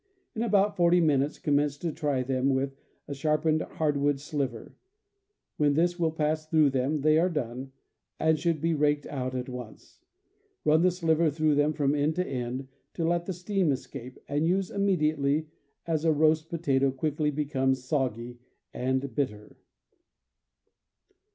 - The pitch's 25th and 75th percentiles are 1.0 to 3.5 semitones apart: Yes, average, 3.0 semitones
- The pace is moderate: Yes, average, 155 wpm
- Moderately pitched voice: Yes, medium, 150 Hz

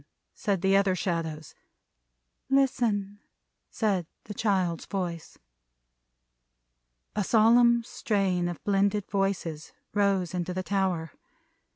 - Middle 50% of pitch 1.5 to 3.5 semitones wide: Yes, average, 2.7 semitones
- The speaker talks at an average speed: No, slow, 95 wpm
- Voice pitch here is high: Yes, high, 195 Hz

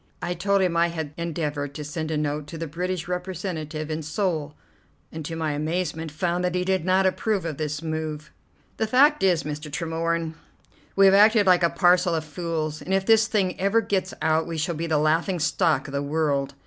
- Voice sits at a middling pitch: Yes, medium, 165 Hz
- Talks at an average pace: No, fast, 210 wpm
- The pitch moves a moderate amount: Yes, average, 3.1 semitones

